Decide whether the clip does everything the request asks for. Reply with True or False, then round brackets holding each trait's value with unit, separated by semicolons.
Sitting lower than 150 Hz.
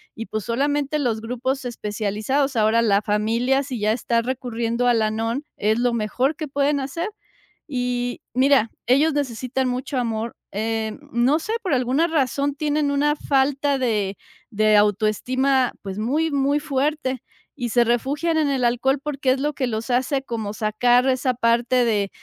False (250 Hz)